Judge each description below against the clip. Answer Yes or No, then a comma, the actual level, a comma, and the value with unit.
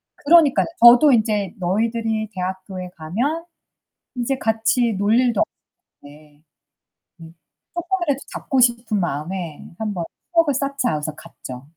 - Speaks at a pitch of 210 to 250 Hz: Yes, high, 220 Hz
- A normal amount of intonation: No, wide, 6.1 semitones